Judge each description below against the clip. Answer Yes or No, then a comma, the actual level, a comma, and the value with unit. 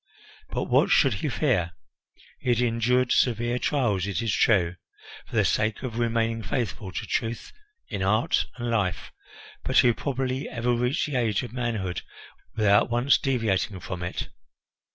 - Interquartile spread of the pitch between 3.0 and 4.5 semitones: Yes, average, 3.4 semitones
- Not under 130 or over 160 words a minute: Yes, average, 155 wpm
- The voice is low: Yes, low, 115 Hz